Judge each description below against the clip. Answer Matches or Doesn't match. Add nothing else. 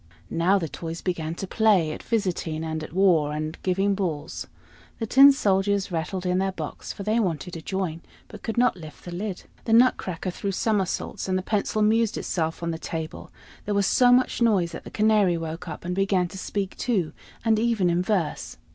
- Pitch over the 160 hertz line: Matches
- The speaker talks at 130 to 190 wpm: Doesn't match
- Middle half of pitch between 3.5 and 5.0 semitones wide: Matches